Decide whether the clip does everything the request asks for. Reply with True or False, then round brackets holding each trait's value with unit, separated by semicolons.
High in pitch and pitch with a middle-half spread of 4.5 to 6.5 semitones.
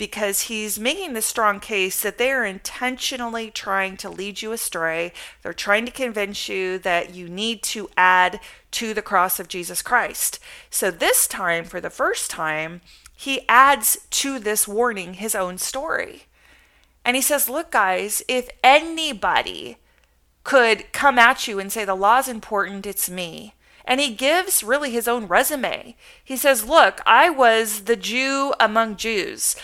True (225 Hz; 5.1 semitones)